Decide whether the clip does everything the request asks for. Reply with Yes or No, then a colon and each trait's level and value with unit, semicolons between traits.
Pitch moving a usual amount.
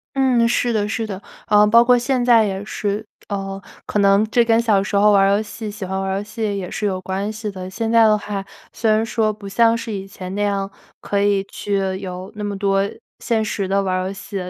No: narrow, 2.3 semitones